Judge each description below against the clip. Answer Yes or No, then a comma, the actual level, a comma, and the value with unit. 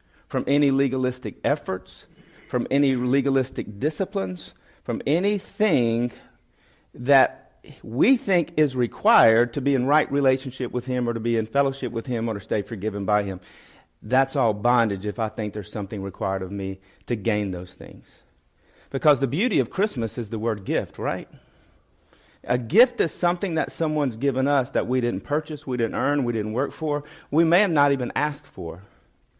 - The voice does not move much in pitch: No, average, 4.8 semitones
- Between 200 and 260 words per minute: No, average, 175 wpm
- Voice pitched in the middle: No, low, 125 Hz